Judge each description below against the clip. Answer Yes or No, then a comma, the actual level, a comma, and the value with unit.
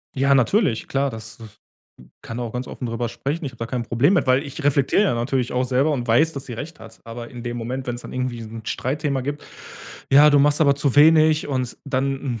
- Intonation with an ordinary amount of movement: Yes, average, 3.3 semitones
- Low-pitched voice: Yes, low, 130 Hz